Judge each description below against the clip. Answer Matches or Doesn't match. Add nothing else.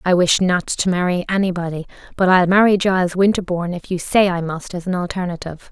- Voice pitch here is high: Doesn't match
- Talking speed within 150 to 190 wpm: Doesn't match